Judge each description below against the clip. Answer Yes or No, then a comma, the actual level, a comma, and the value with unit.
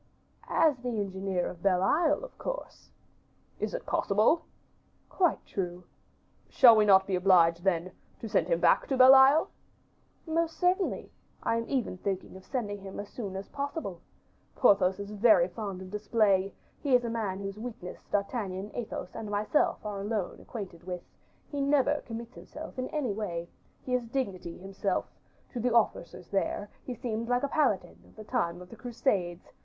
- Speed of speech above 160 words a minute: Yes, average, 170 wpm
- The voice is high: Yes, high, 210 Hz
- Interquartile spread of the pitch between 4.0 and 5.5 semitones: Yes, average, 4.9 semitones